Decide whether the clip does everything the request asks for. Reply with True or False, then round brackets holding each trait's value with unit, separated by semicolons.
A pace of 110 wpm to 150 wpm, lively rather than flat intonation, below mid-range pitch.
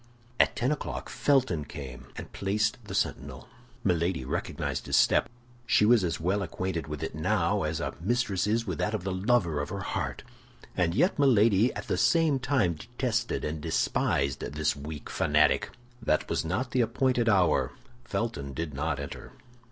False (170 wpm; 7.0 semitones; 95 Hz)